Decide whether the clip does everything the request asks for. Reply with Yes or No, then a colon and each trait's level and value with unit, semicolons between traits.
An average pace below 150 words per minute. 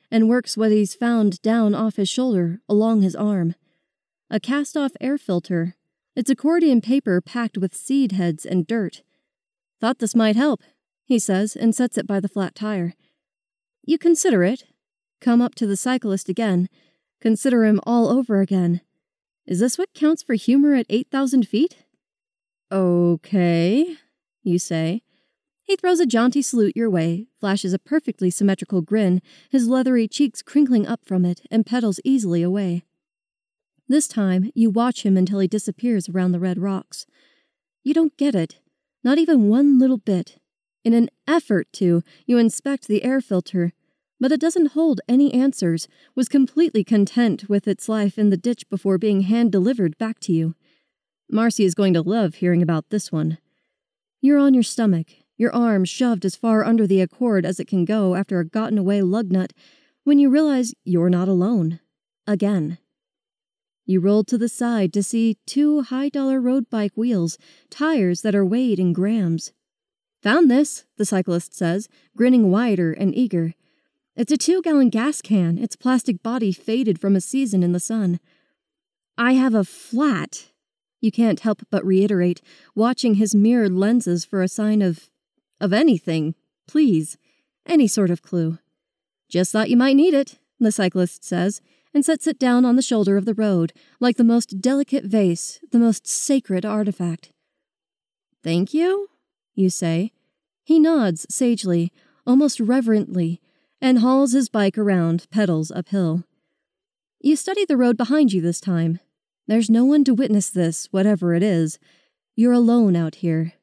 No: average, 165 wpm